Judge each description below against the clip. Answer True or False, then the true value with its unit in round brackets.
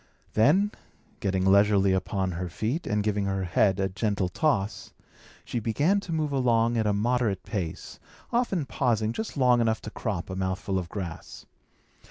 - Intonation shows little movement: False (4.4 semitones)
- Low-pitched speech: True (105 Hz)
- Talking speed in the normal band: True (165 wpm)